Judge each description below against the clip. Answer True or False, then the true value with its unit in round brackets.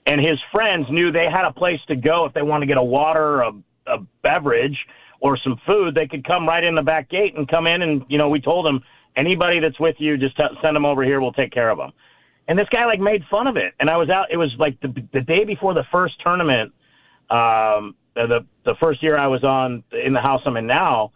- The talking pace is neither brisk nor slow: False (260 wpm)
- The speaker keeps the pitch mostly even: False (3.6 semitones)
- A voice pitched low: False (155 Hz)